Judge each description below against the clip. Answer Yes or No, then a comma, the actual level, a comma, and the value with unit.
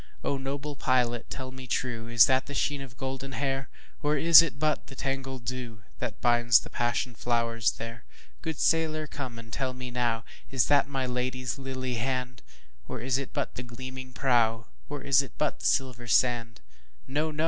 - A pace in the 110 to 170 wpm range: Yes, average, 160 wpm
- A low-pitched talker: Yes, low, 130 Hz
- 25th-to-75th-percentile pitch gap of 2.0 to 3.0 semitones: Yes, narrow, 2.4 semitones